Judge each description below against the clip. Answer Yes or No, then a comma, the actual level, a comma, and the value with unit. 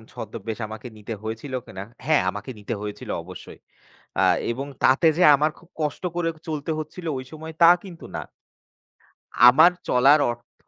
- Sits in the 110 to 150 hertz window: Yes, low, 135 Hz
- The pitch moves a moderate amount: No, wide, 5.8 semitones